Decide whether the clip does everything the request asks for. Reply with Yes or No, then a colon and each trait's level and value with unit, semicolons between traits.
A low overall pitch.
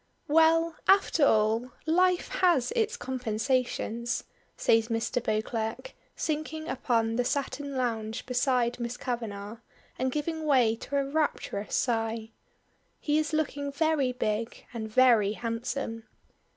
No: very high, 250 Hz